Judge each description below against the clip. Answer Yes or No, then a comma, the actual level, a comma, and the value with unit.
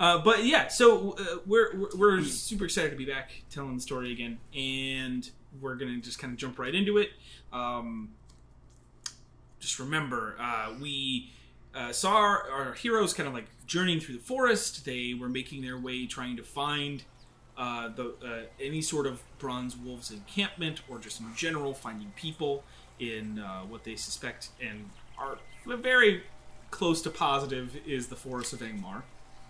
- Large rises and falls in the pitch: No, average, 4.9 semitones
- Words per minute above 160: Yes, average, 170 wpm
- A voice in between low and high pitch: No, low, 130 Hz